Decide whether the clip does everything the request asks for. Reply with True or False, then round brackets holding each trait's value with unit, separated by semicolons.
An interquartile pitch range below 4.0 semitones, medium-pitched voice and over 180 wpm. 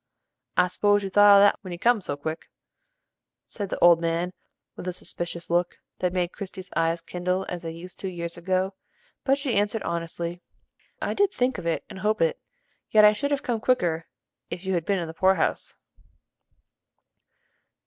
True (3.3 semitones; 180 Hz; 190 wpm)